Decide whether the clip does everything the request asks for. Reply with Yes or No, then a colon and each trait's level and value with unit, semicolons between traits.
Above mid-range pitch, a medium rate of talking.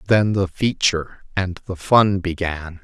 No: very low, 95 Hz; average, 150 wpm